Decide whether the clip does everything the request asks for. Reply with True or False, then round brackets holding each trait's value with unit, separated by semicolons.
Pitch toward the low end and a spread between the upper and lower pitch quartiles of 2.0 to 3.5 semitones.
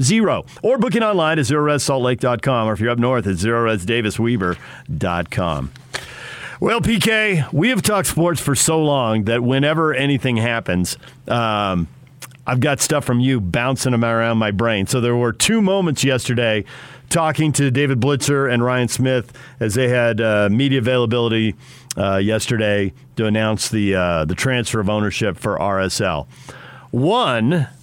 False (125 Hz; 4.1 semitones)